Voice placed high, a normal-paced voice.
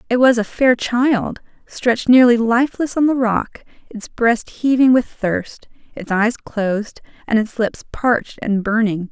Yes: high, 235 Hz; average, 165 wpm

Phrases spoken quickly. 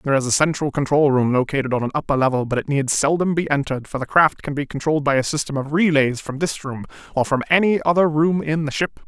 Yes: fast, 260 wpm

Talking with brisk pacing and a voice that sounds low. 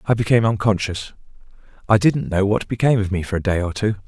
Yes: fast, 220 wpm; low, 105 Hz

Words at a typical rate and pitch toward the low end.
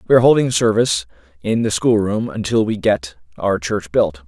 Yes: average, 180 wpm; low, 100 Hz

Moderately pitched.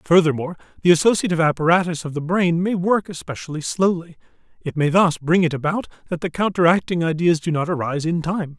Yes: medium, 170 Hz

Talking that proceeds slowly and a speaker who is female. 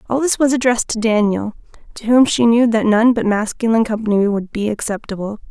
No: average, 195 wpm; female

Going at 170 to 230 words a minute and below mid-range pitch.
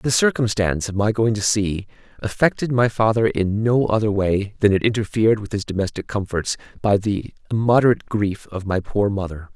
Yes: average, 180 wpm; low, 105 Hz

